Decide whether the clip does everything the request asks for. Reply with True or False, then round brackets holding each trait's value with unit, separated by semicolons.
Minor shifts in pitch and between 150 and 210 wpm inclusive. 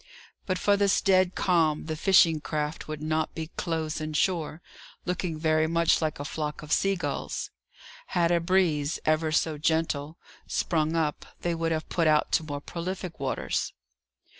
True (2.1 semitones; 165 wpm)